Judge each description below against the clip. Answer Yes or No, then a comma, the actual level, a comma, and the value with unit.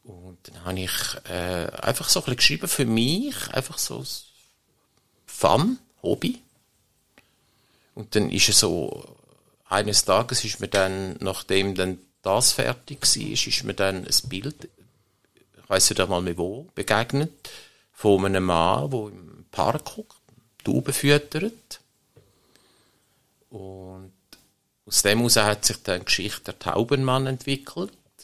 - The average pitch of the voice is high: No, low, 105 Hz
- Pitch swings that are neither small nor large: No, wide, 6.2 semitones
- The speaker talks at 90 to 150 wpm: Yes, average, 130 wpm